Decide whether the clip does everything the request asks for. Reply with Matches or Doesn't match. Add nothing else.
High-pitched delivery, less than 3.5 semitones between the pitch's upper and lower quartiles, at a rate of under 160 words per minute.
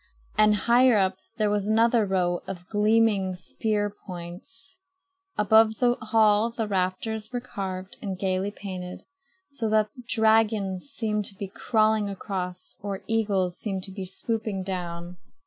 Matches